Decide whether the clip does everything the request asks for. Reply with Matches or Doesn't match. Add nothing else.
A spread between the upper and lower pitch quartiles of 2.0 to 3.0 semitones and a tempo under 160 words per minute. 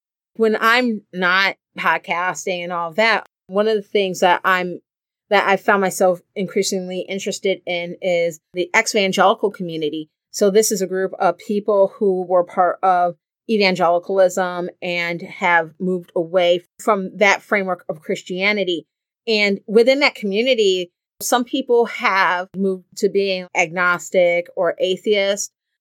Matches